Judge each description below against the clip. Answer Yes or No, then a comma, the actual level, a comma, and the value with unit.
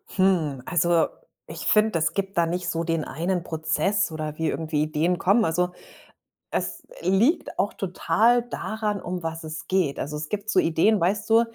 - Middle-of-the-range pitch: Yes, medium, 175 Hz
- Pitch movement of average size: Yes, average, 4.0 semitones